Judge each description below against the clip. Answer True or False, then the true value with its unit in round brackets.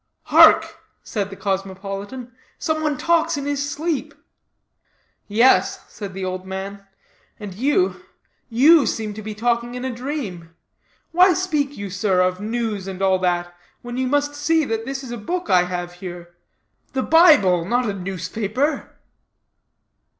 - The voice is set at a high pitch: True (220 Hz)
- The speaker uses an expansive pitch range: True (6.8 semitones)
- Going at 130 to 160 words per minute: True (150 wpm)